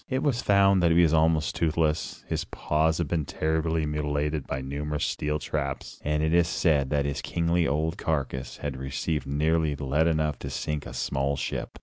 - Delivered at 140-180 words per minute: No, average, 190 wpm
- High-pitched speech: No, very low, 75 Hz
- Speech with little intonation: Yes, narrow, 2.2 semitones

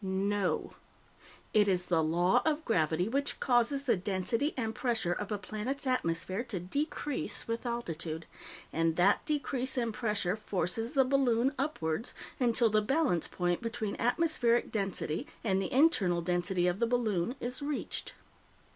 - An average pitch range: No, wide, 5.9 semitones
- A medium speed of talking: Yes, average, 145 wpm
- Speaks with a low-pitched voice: No, high, 220 Hz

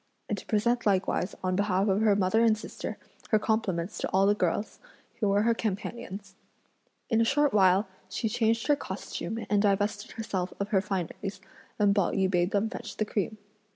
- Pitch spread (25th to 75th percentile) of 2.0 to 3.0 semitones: Yes, narrow, 2.5 semitones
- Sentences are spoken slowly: No, average, 190 wpm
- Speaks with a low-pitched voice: No, high, 205 Hz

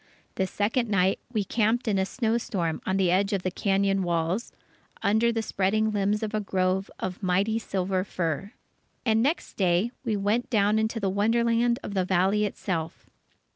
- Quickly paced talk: No, average, 175 wpm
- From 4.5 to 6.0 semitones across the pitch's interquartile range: No, average, 2.7 semitones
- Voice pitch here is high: Yes, high, 200 Hz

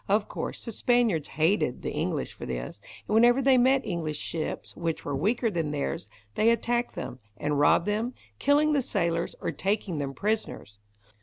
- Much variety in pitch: Yes, wide, 7.5 semitones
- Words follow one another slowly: No, average, 175 wpm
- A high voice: Yes, high, 200 Hz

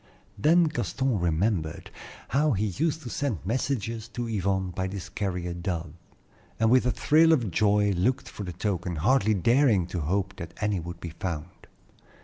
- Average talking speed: Yes, average, 165 wpm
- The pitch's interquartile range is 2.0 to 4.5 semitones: No, wide, 5.4 semitones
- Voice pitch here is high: No, low, 100 Hz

